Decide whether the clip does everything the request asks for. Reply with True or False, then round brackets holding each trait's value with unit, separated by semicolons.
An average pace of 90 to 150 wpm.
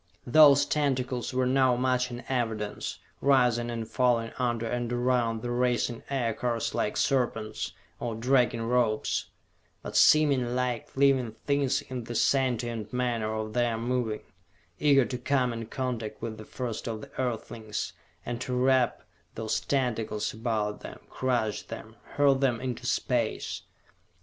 True (140 wpm)